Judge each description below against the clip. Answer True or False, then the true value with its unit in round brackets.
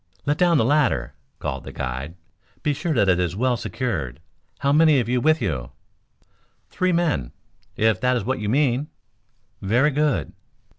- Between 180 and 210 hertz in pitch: False (125 Hz)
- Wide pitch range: True (8.2 semitones)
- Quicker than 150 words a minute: True (165 wpm)